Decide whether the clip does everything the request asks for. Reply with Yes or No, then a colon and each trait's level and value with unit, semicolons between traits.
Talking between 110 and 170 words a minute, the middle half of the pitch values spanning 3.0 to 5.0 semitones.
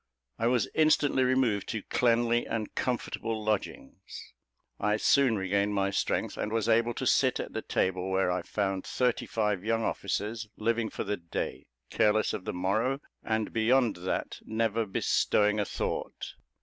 No: average, 160 wpm; narrow, 2.6 semitones